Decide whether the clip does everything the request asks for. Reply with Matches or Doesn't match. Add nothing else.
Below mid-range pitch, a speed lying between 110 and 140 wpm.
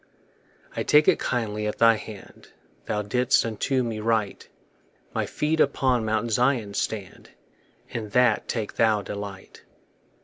Matches